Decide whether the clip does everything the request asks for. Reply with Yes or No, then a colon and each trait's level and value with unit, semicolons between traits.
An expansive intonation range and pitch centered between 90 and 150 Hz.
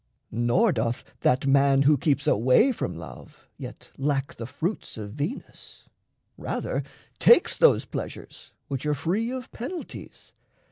Yes: wide, 8.7 semitones; medium, 140 Hz